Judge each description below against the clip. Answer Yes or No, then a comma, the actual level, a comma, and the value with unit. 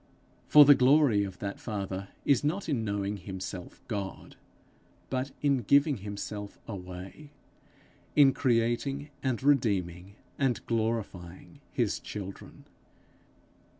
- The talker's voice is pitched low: Yes, low, 110 Hz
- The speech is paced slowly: Yes, slow, 110 wpm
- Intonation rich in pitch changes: Yes, wide, 5.7 semitones